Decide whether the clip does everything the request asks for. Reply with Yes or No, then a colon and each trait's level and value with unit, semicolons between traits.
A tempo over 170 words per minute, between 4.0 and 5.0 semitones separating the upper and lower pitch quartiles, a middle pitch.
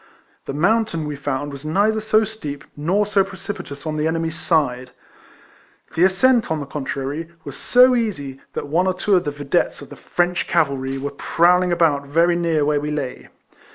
Yes: average, 185 wpm; average, 4.6 semitones; medium, 160 Hz